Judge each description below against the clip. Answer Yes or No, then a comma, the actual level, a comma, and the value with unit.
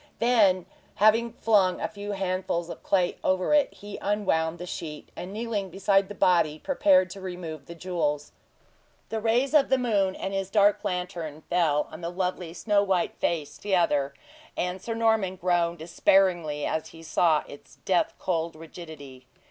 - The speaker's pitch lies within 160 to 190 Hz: Yes, medium, 185 Hz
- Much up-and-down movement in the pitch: No, average, 3.4 semitones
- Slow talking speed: No, average, 165 wpm